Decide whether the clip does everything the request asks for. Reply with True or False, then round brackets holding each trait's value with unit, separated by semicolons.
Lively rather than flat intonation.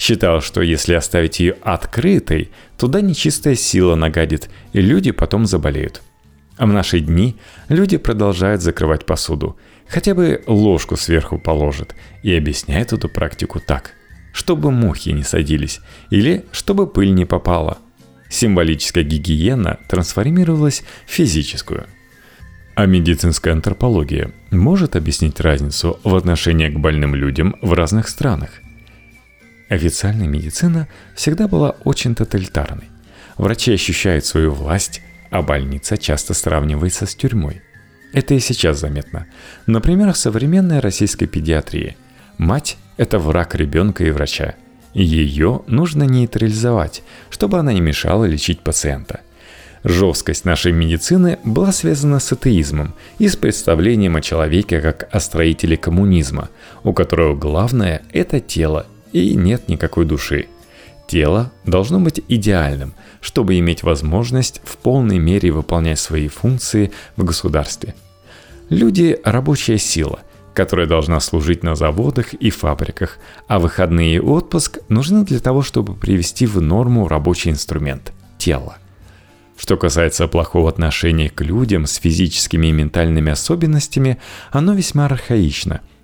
True (6.0 semitones)